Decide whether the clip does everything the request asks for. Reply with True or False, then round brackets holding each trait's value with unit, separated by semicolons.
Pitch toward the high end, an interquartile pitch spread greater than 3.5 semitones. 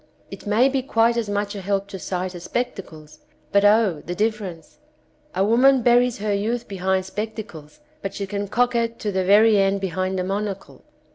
False (200 Hz; 3.2 semitones)